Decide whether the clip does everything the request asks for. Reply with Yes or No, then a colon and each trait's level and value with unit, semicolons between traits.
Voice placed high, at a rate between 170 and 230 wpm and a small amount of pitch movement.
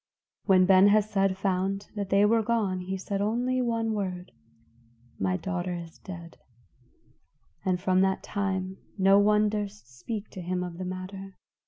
No: high, 195 Hz; average, 155 wpm; narrow, 2.0 semitones